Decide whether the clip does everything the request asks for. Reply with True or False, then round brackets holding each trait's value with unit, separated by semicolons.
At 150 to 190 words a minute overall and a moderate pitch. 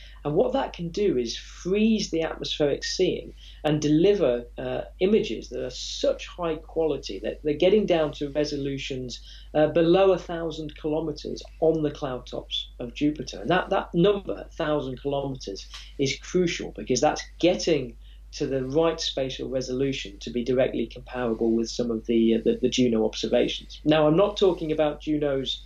True (165 wpm; 150 Hz)